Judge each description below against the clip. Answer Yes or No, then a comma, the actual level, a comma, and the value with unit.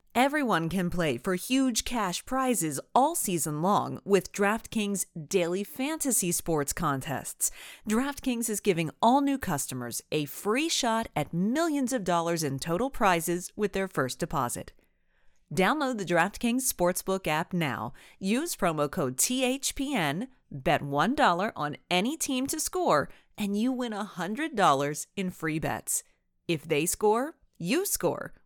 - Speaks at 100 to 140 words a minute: Yes, slow, 135 wpm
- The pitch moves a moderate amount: No, wide, 7.5 semitones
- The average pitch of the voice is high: Yes, high, 195 Hz